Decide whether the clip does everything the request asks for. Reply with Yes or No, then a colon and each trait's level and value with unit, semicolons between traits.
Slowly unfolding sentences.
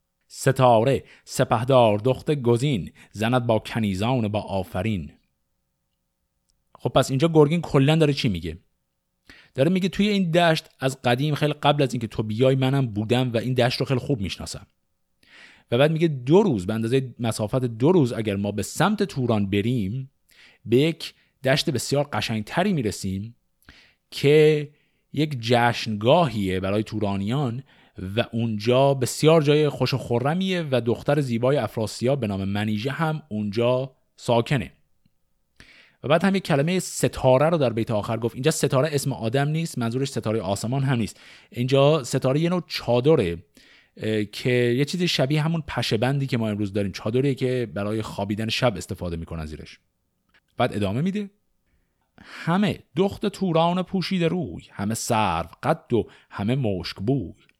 No: average, 150 wpm